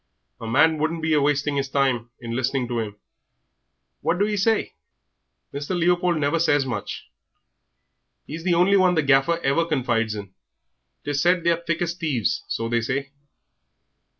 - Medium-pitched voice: Yes, medium, 145 Hz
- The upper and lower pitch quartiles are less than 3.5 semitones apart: No, average, 4.9 semitones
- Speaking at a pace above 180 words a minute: No, average, 175 wpm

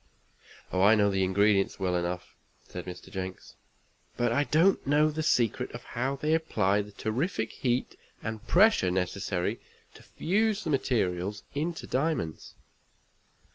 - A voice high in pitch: No, low, 110 Hz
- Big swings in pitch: Yes, wide, 8.0 semitones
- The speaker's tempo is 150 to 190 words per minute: No, average, 140 wpm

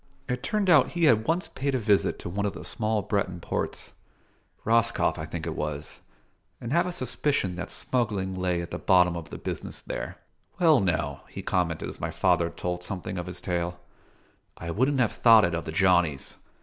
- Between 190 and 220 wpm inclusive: Yes, average, 200 wpm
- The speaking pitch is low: Yes, very low, 95 Hz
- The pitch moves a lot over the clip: Yes, wide, 6.0 semitones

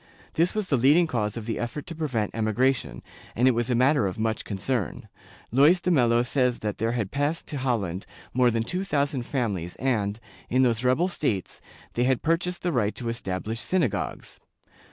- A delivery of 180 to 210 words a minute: Yes, average, 190 wpm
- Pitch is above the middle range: No, low, 125 Hz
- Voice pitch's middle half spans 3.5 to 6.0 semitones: Yes, average, 4.5 semitones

